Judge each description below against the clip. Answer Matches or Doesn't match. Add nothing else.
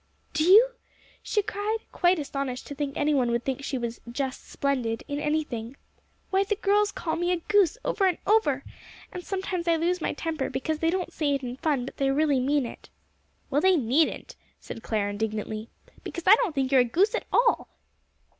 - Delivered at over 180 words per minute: Matches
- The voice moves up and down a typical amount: Doesn't match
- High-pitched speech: Matches